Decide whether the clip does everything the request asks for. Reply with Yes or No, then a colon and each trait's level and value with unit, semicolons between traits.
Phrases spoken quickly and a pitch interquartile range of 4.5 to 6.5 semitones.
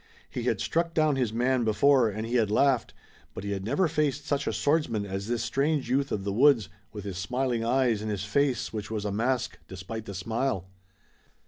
Yes: fast, 210 wpm; average, 4.9 semitones